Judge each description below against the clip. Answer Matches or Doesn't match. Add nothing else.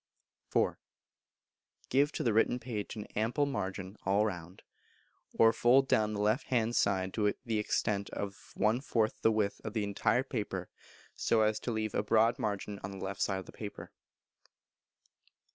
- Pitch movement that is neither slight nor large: Doesn't match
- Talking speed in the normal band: Matches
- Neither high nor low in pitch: Doesn't match